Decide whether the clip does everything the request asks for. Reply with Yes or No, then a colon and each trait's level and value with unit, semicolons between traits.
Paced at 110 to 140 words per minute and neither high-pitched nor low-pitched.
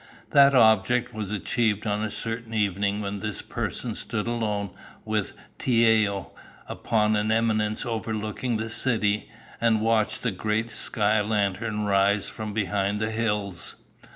No: slow, 135 wpm; low, 110 Hz